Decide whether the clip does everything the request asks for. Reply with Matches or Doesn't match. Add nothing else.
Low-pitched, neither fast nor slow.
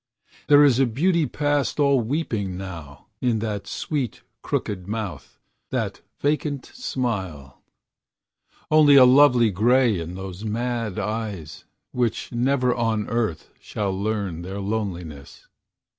Doesn't match